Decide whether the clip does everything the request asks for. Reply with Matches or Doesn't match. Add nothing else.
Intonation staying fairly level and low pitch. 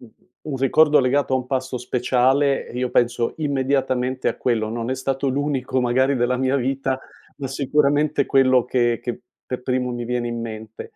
Matches